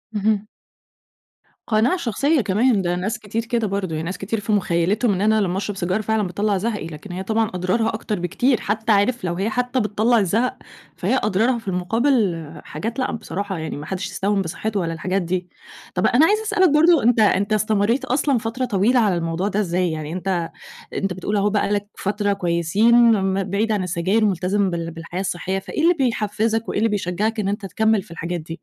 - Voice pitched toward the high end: Yes, high, 205 Hz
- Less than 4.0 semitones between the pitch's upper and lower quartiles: Yes, average, 3.5 semitones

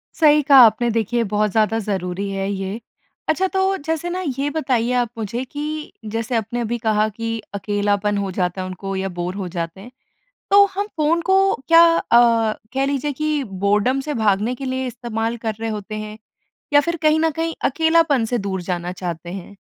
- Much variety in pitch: Yes, wide, 6.4 semitones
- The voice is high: Yes, high, 230 Hz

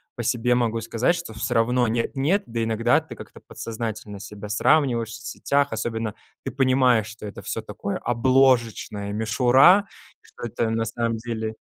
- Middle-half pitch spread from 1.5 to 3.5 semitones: Yes, narrow, 2.4 semitones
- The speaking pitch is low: Yes, low, 115 Hz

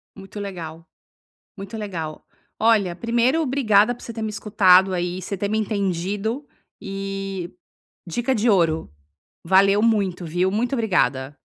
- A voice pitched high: Yes, high, 195 Hz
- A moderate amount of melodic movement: Yes, average, 3.5 semitones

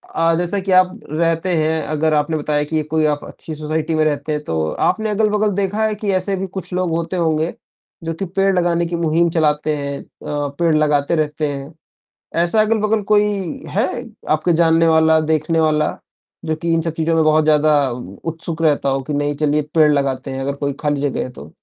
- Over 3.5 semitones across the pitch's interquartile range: No, narrow, 2.4 semitones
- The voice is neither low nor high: Yes, medium, 160 Hz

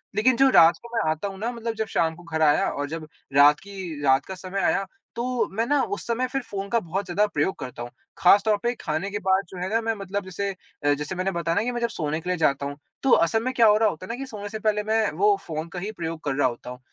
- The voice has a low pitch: No, high, 190 Hz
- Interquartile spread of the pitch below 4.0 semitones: No, wide, 5.5 semitones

